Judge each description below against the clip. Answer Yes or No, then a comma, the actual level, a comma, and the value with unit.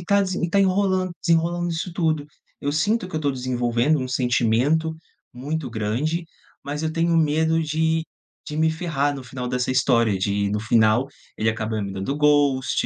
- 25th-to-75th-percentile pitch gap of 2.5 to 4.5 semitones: No, average, 5.0 semitones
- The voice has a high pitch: No, medium, 145 Hz